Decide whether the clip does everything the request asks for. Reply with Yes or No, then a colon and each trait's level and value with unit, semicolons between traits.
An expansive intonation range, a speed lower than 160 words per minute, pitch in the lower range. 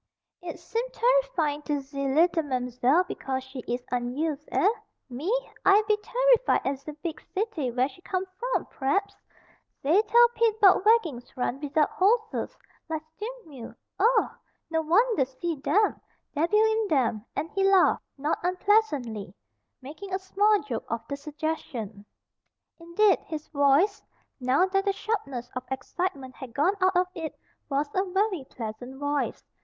No: wide, 6.9 semitones; average, 150 wpm; very high, 320 Hz